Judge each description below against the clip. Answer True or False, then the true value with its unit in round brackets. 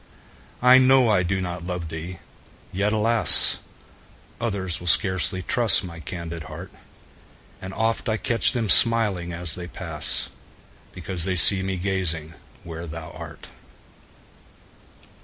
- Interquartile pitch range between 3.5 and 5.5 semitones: True (3.9 semitones)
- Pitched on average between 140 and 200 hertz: False (95 Hz)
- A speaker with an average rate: False (130 wpm)